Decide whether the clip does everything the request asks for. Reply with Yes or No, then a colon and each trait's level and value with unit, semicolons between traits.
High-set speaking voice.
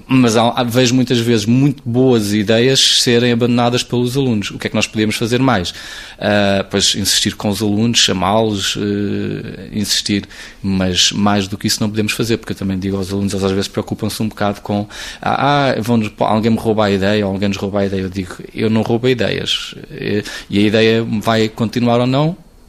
No: low, 110 Hz